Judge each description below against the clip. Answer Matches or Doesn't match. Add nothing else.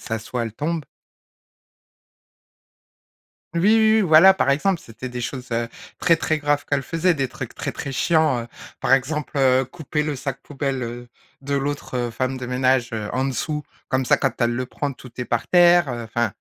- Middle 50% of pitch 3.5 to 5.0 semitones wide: Matches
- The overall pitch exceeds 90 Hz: Matches